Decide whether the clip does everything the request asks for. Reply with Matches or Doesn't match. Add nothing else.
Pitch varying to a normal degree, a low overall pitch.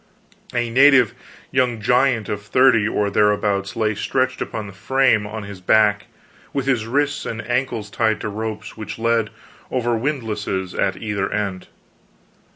Matches